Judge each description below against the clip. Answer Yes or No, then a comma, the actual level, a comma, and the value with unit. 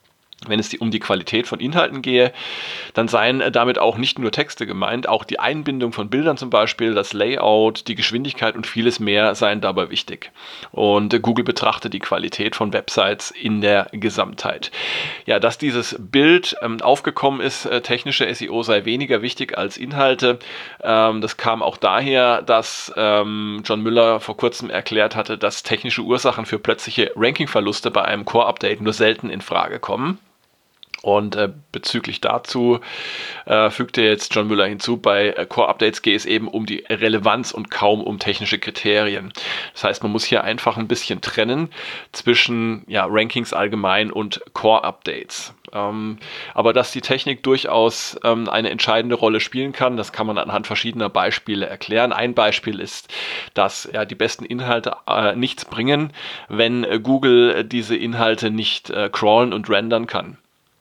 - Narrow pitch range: Yes, narrow, 2.3 semitones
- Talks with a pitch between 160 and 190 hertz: No, low, 115 Hz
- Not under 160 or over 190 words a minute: Yes, average, 165 wpm